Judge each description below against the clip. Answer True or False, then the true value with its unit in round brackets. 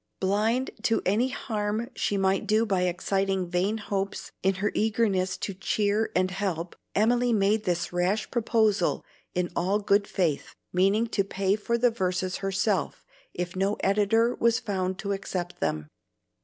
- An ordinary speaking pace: True (155 wpm)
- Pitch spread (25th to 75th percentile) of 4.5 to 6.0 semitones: False (2.6 semitones)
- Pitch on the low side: False (195 Hz)